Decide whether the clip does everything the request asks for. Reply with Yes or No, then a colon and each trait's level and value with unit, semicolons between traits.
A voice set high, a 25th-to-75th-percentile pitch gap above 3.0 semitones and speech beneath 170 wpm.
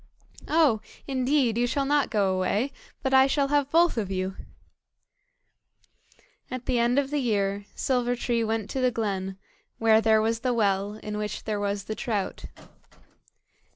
Yes: high, 230 Hz; average, 4.4 semitones; average, 160 wpm